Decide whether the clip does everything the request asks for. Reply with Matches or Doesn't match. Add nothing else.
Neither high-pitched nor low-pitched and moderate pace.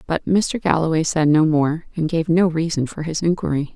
Doesn't match